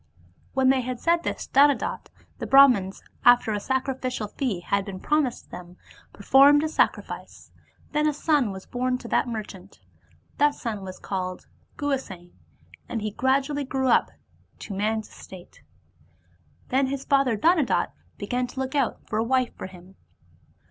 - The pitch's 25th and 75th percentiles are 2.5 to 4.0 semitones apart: No, average, 5.2 semitones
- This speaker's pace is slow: No, average, 155 wpm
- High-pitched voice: Yes, very high, 250 Hz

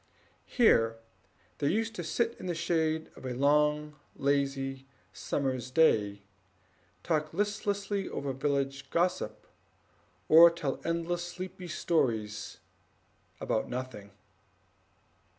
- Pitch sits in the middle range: Yes, medium, 150 Hz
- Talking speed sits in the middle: No, slow, 100 wpm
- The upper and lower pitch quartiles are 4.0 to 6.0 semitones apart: Yes, average, 4.6 semitones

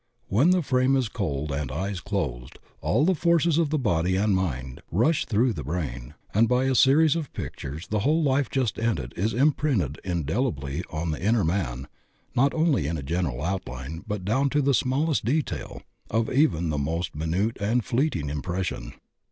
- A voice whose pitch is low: Yes, low, 100 Hz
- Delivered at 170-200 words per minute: Yes, average, 185 wpm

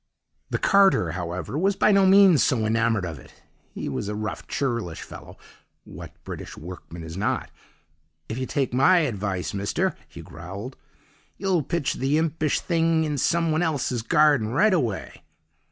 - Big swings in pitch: Yes, wide, 8.4 semitones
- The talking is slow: No, average, 155 wpm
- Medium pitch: No, low, 130 Hz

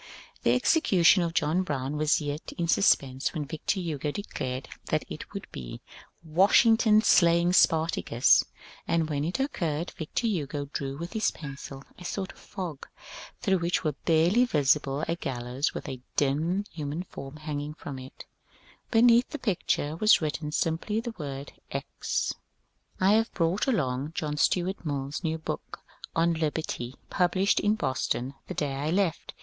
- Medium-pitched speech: Yes, medium, 160 Hz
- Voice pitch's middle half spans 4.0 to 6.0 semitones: Yes, average, 4.5 semitones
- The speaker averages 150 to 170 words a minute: Yes, average, 160 wpm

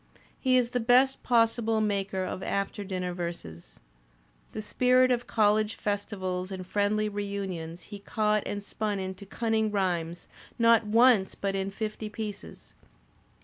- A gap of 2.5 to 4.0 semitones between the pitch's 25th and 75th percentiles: Yes, average, 2.8 semitones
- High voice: Yes, high, 205 Hz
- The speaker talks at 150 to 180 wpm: No, average, 140 wpm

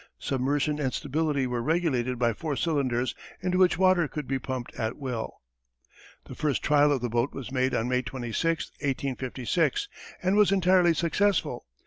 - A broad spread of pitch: No, average, 4.7 semitones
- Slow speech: No, average, 160 wpm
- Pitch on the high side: No, medium, 140 Hz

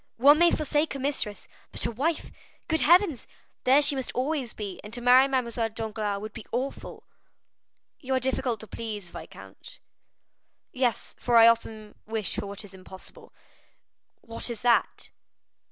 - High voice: Yes, high, 235 Hz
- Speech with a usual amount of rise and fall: Yes, average, 3.9 semitones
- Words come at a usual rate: Yes, average, 155 wpm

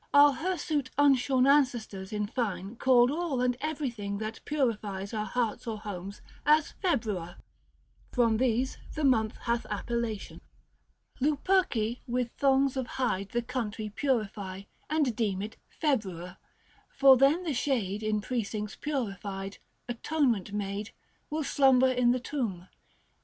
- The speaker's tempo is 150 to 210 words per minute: No, slow, 135 wpm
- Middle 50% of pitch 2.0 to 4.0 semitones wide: No, average, 4.7 semitones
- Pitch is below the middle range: No, high, 240 Hz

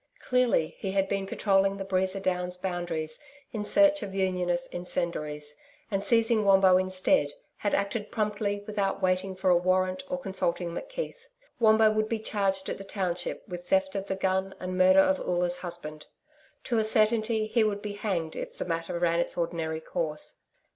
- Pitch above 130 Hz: Yes, high, 190 Hz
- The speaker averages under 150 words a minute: No, average, 175 wpm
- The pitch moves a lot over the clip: No, average, 2.8 semitones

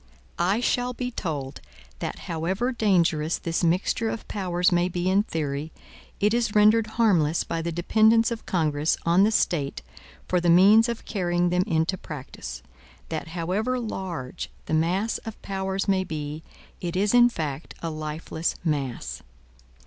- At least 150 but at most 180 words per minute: Yes, average, 155 wpm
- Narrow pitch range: No, average, 4.8 semitones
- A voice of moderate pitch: Yes, medium, 180 Hz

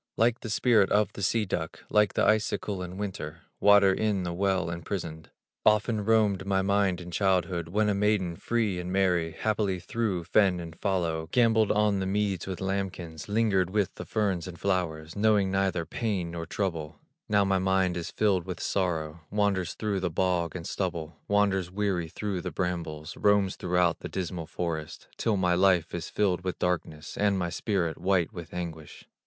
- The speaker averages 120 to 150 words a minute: No, average, 180 wpm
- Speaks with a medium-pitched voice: No, very low, 95 Hz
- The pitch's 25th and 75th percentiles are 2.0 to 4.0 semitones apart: Yes, average, 2.9 semitones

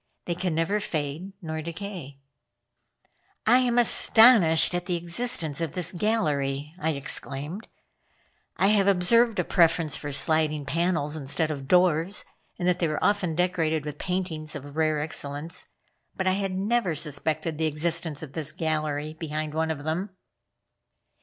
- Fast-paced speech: No, average, 150 wpm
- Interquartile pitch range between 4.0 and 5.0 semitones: No, average, 3.4 semitones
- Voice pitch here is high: No, medium, 160 Hz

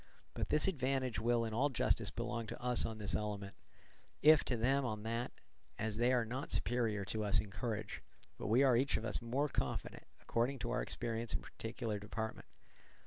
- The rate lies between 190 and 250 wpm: Yes, average, 200 wpm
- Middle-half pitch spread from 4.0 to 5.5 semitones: No, average, 2.7 semitones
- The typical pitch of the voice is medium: No, low, 115 Hz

